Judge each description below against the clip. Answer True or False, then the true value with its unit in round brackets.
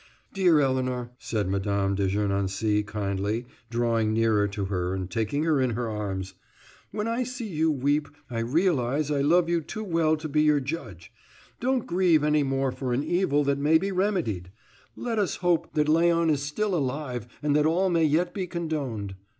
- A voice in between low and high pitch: True (145 Hz)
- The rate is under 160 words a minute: False (185 wpm)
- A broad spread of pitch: True (7.2 semitones)